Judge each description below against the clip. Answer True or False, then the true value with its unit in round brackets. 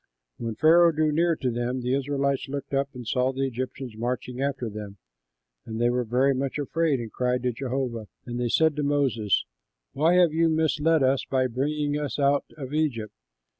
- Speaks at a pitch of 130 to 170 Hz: True (135 Hz)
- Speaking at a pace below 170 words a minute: False (190 wpm)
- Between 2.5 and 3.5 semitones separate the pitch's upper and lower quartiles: True (3.2 semitones)